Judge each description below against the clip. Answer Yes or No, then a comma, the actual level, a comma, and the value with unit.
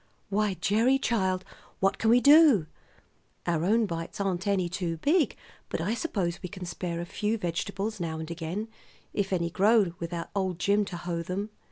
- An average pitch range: Yes, average, 3.7 semitones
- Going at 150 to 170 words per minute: No, average, 180 wpm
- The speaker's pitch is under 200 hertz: Yes, high, 190 Hz